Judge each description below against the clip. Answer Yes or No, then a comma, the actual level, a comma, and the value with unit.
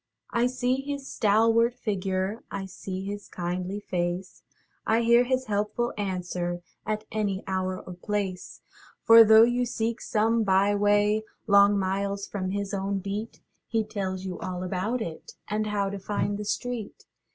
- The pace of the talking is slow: No, average, 155 wpm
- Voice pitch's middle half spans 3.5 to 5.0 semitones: No, average, 2.8 semitones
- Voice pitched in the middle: No, high, 205 Hz